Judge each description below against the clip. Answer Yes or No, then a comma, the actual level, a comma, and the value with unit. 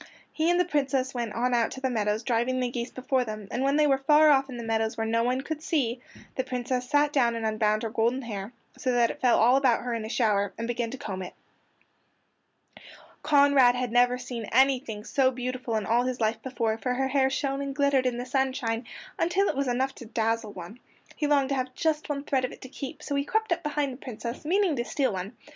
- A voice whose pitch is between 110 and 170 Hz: No, very high, 255 Hz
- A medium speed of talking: No, fast, 240 wpm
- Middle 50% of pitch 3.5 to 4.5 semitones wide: No, average, 3.0 semitones